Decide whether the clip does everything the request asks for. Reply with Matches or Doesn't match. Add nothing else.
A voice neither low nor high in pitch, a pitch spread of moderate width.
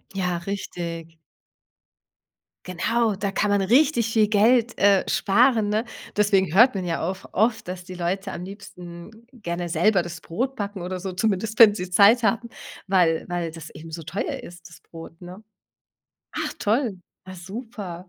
Doesn't match